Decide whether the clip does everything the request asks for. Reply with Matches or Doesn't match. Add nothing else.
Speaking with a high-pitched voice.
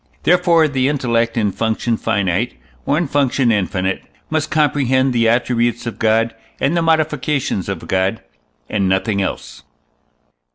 Doesn't match